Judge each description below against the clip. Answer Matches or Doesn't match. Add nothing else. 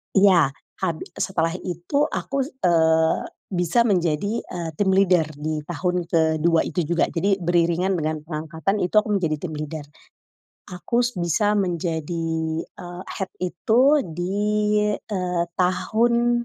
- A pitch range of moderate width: Matches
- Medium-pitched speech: Matches